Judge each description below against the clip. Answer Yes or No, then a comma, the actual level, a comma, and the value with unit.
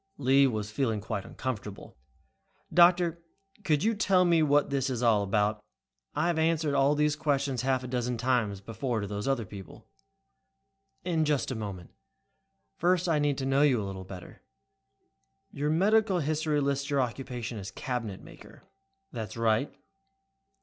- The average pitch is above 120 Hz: Yes, low, 135 Hz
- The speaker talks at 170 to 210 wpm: No, average, 155 wpm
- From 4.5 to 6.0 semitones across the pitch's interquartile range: Yes, wide, 5.5 semitones